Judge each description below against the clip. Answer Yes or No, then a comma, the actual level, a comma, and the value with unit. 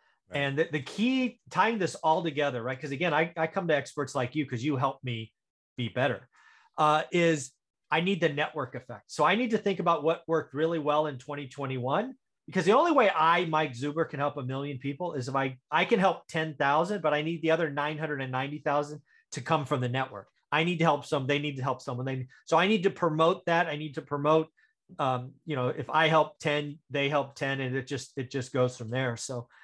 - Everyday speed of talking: No, fast, 240 wpm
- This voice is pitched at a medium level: Yes, medium, 150 Hz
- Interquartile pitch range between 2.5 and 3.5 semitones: Yes, average, 3.1 semitones